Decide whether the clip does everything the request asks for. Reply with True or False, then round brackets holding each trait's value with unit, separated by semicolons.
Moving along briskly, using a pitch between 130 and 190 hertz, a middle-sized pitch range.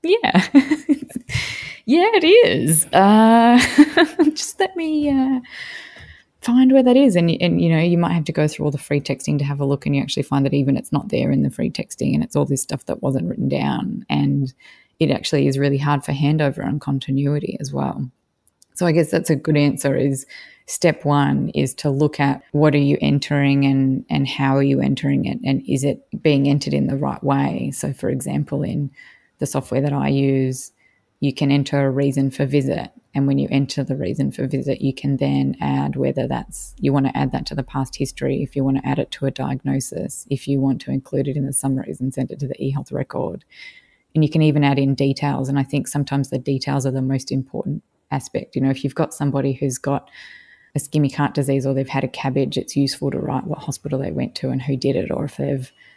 False (230 wpm; 140 Hz; 2.1 semitones)